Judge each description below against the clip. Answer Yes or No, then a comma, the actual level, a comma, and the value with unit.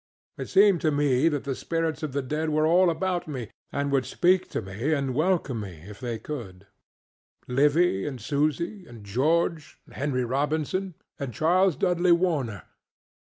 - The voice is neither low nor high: Yes, medium, 150 Hz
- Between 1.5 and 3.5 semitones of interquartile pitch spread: No, average, 5.0 semitones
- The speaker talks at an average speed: Yes, average, 165 wpm